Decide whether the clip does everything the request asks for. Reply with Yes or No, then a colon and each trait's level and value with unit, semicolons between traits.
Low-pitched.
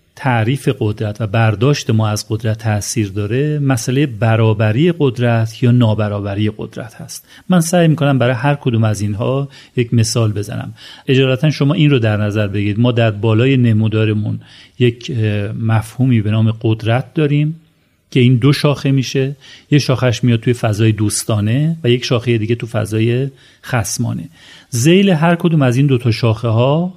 Yes: low, 120 Hz